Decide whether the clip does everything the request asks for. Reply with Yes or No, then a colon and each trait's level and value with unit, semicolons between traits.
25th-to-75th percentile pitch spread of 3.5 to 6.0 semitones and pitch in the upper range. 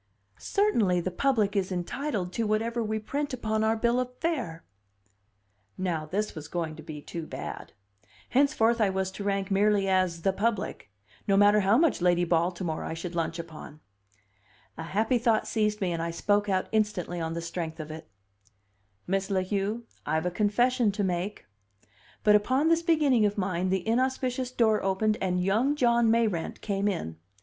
Yes: average, 4.4 semitones; high, 200 Hz